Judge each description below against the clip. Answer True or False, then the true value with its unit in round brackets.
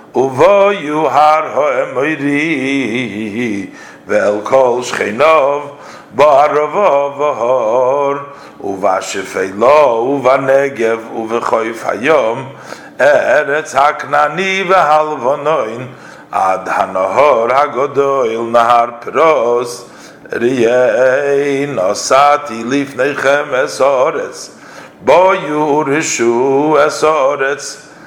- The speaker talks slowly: True (85 wpm)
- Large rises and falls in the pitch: False (3.8 semitones)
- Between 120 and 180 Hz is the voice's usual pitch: True (140 Hz)